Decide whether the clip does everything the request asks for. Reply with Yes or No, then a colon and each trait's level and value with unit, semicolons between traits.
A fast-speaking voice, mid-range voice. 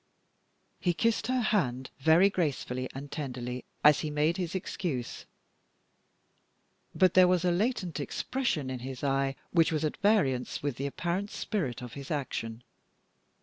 No: average, 145 wpm; medium, 150 Hz